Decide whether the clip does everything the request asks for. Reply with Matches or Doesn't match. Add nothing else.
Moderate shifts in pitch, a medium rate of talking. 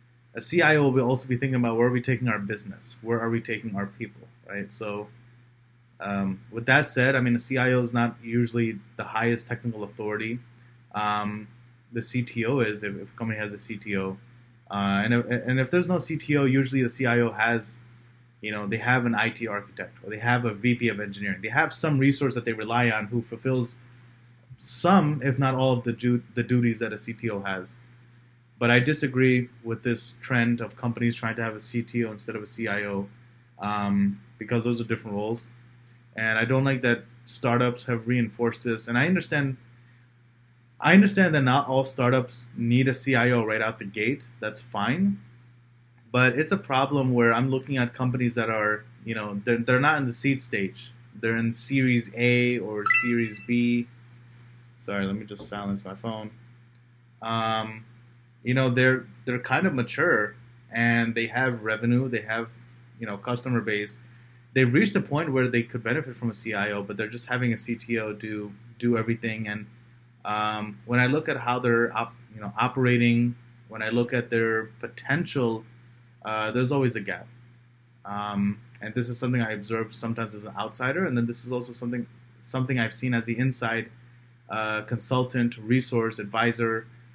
Doesn't match